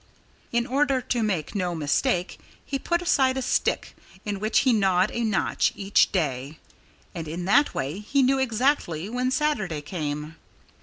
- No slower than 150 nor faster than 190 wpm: Yes, average, 160 wpm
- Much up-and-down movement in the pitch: Yes, wide, 7.4 semitones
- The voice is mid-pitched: No, high, 210 Hz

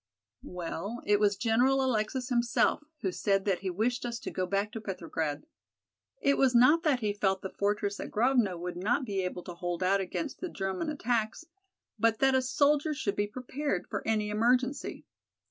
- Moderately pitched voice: No, high, 215 Hz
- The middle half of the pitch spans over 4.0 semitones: Yes, average, 4.7 semitones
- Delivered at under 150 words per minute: No, average, 185 wpm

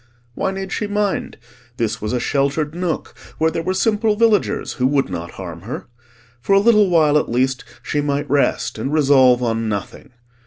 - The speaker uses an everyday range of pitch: No, wide, 7.4 semitones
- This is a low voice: No, medium, 145 Hz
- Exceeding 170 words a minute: Yes, average, 185 wpm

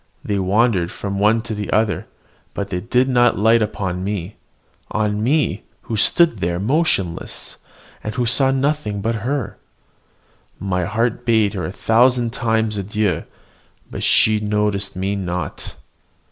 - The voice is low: Yes, low, 105 Hz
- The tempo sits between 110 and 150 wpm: Yes, average, 145 wpm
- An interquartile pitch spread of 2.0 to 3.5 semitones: Yes, average, 3.1 semitones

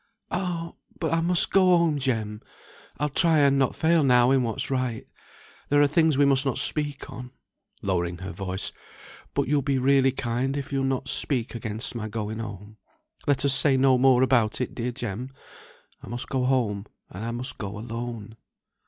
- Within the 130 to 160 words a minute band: No, average, 185 wpm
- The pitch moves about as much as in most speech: Yes, average, 3.7 semitones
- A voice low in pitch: Yes, low, 130 Hz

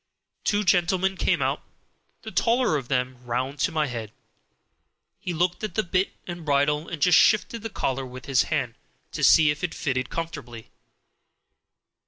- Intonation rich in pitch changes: Yes, wide, 5.7 semitones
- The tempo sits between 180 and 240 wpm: No, average, 170 wpm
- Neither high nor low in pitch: Yes, medium, 155 Hz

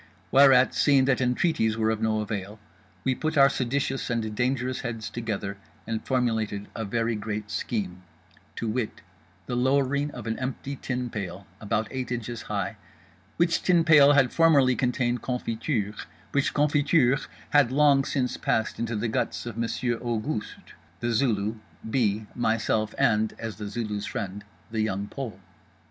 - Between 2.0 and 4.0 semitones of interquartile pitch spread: Yes, average, 3.6 semitones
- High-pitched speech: No, low, 120 Hz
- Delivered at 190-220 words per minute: No, average, 150 wpm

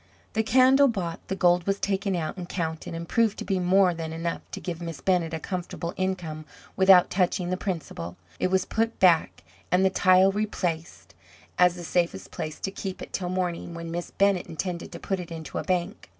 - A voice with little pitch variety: Yes, narrow, 2.3 semitones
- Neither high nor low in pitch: Yes, medium, 180 Hz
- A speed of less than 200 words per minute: No, fast, 205 wpm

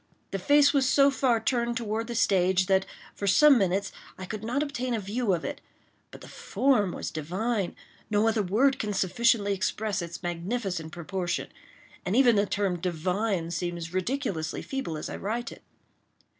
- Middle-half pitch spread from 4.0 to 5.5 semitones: Yes, average, 4.8 semitones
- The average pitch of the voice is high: Yes, high, 205 Hz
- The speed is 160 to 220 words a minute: Yes, average, 165 wpm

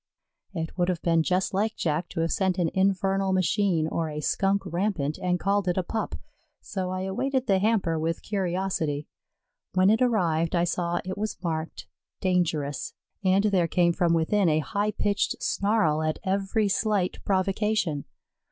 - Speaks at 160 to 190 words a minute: Yes, average, 165 wpm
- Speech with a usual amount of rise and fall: Yes, average, 3.2 semitones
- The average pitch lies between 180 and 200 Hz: Yes, medium, 185 Hz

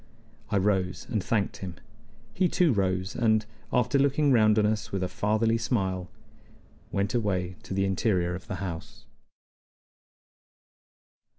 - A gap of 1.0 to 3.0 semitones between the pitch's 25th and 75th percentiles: No, average, 3.4 semitones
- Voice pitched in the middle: No, low, 100 Hz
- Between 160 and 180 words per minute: No, slow, 135 wpm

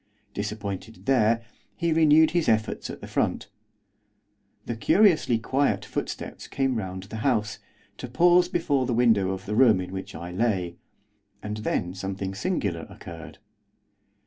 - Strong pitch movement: Yes, wide, 5.7 semitones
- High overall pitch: No, low, 110 Hz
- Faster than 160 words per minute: No, average, 145 wpm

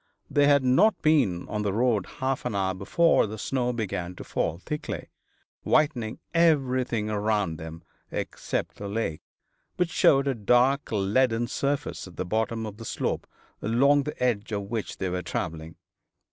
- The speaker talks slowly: No, average, 160 wpm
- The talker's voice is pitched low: Yes, low, 115 Hz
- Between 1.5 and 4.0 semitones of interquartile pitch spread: No, average, 5.2 semitones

